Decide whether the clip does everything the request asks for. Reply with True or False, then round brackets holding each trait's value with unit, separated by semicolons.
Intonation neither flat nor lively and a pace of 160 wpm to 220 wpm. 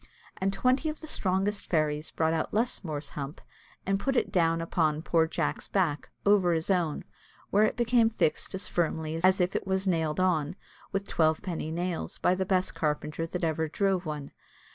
True (3.5 semitones; 180 wpm)